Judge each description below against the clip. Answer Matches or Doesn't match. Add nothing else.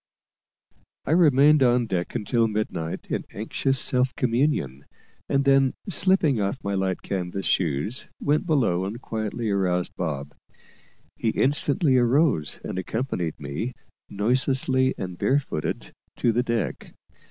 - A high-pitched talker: Doesn't match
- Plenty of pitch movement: Matches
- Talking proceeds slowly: Matches